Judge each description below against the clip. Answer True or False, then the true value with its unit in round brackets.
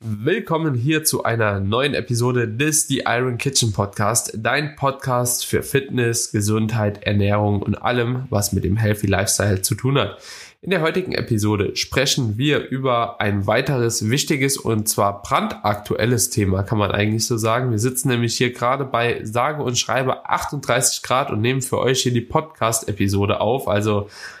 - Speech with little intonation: False (3.7 semitones)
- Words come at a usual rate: True (160 wpm)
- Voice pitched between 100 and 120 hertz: True (115 Hz)